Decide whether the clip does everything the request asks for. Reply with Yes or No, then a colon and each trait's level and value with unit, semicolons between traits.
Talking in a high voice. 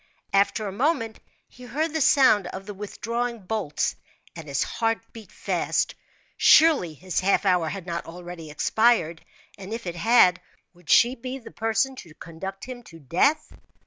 Yes: high, 205 Hz